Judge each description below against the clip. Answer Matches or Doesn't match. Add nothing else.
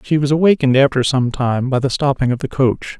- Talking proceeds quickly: Matches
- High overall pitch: Doesn't match